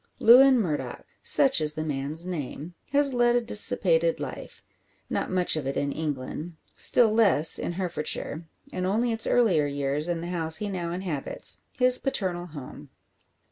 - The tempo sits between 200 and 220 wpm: No, average, 160 wpm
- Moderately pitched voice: Yes, medium, 175 Hz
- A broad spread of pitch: Yes, wide, 7.1 semitones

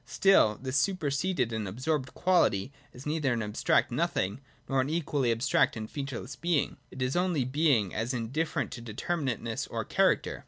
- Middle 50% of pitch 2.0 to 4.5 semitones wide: No, average, 5.1 semitones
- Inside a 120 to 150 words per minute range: No, average, 165 wpm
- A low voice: Yes, low, 130 Hz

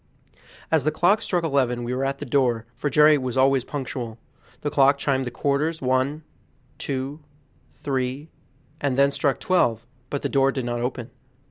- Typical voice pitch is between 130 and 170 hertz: Yes, low, 135 Hz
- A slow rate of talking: No, average, 170 wpm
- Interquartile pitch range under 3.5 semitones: Yes, narrow, 2.4 semitones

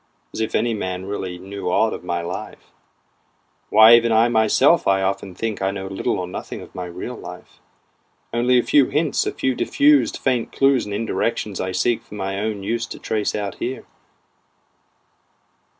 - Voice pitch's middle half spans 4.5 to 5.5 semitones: No, average, 3.6 semitones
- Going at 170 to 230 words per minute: Yes, average, 175 wpm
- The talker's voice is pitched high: No, low, 105 Hz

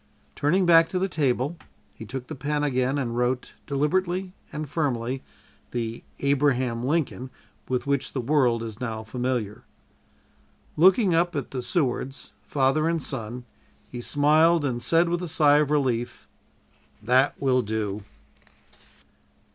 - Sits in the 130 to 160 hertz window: Yes, low, 135 Hz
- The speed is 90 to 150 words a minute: Yes, average, 140 wpm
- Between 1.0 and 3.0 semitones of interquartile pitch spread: No, average, 4.1 semitones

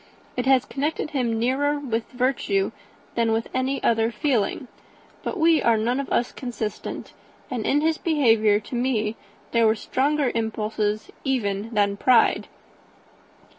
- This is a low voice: No, high, 240 Hz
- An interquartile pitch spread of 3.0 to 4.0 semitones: Yes, average, 3.5 semitones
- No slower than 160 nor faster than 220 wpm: No, slow, 135 wpm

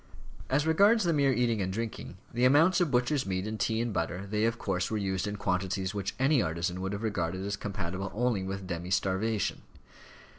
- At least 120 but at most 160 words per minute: No, average, 200 wpm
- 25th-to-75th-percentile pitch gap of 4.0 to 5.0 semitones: Yes, average, 4.6 semitones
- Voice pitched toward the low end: Yes, low, 105 Hz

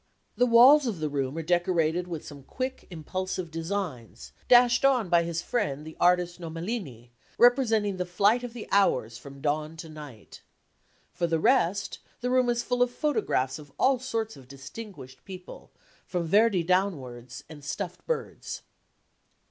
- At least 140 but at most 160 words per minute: Yes, average, 155 wpm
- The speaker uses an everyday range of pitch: No, wide, 7.0 semitones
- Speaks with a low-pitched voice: No, medium, 180 Hz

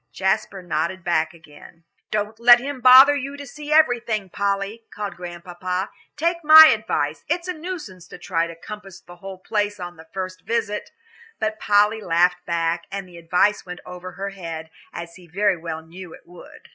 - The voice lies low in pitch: No, high, 190 Hz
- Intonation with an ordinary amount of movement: Yes, average, 4.1 semitones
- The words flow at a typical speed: Yes, average, 180 wpm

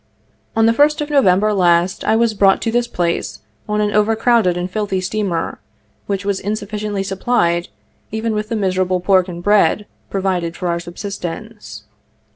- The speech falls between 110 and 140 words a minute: No, average, 170 wpm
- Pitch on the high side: Yes, high, 200 Hz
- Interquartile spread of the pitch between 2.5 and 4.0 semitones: Yes, average, 3.0 semitones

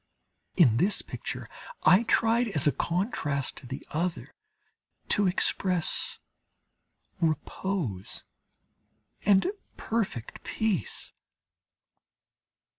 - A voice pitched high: No, medium, 180 Hz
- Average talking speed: No, slow, 80 wpm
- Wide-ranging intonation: Yes, wide, 5.9 semitones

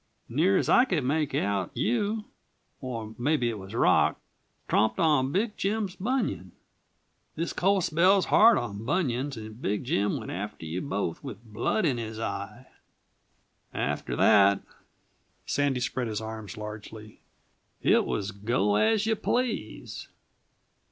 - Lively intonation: Yes, wide, 9.0 semitones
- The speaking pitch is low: Yes, low, 120 Hz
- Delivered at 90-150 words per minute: Yes, average, 140 wpm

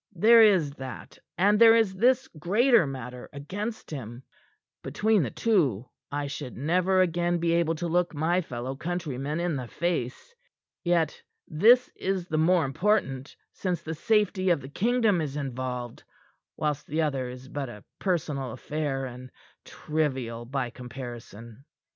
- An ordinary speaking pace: Yes, average, 150 wpm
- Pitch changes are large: Yes, wide, 5.7 semitones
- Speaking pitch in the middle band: Yes, medium, 155 Hz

